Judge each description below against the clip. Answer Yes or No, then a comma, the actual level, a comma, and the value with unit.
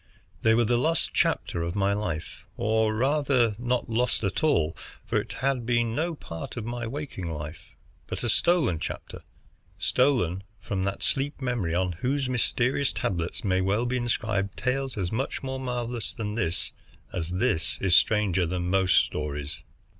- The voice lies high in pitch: No, low, 110 Hz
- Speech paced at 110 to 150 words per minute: No, average, 165 wpm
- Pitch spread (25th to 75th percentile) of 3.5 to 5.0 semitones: No, wide, 5.4 semitones